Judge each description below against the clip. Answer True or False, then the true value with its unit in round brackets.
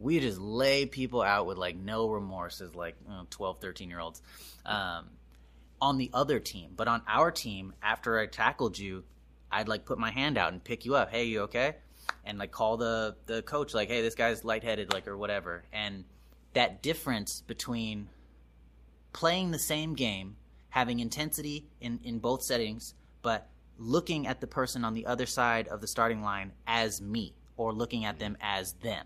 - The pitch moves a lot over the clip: False (4.6 semitones)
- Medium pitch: False (110 Hz)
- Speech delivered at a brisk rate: False (185 wpm)